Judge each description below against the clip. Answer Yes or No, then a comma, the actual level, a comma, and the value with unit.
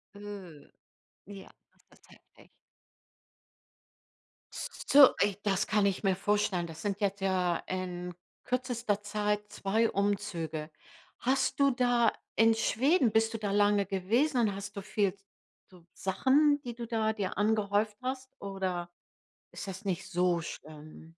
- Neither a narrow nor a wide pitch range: Yes, average, 3.0 semitones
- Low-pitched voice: No, high, 205 Hz